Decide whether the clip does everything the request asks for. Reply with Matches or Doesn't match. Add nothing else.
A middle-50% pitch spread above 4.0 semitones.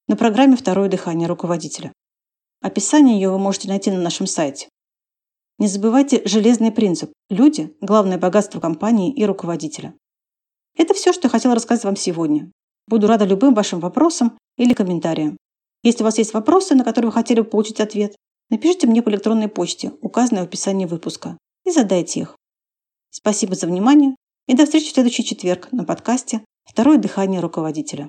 Matches